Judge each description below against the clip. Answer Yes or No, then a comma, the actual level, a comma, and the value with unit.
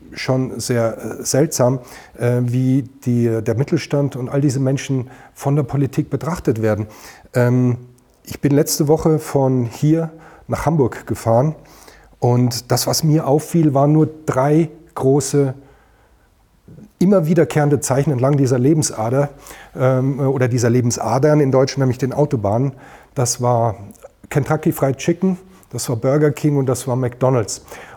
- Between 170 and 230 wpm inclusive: No, average, 130 wpm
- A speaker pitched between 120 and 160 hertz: Yes, low, 135 Hz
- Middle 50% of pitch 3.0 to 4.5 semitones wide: Yes, average, 3.4 semitones